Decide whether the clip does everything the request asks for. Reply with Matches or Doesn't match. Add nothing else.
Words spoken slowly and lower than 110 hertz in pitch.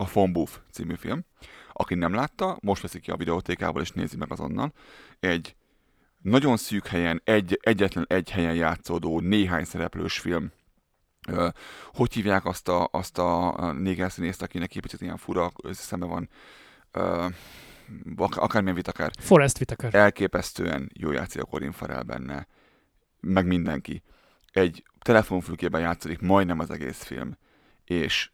Doesn't match